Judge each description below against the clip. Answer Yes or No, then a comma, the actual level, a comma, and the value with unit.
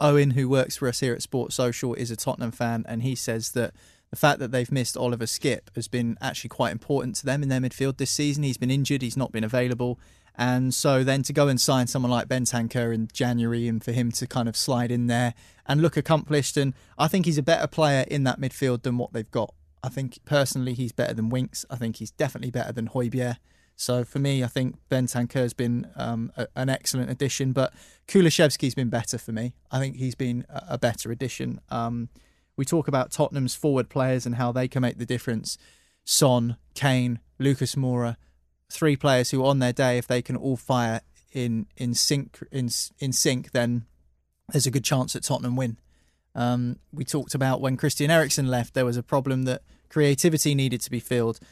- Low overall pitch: Yes, low, 125 Hz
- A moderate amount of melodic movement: No, narrow, 2.3 semitones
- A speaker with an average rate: No, fast, 215 wpm